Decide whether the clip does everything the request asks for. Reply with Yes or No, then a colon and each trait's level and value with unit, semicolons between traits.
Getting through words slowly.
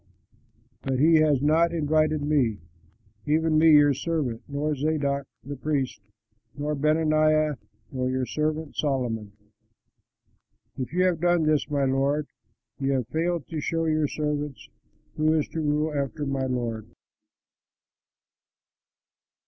Yes: slow, 125 wpm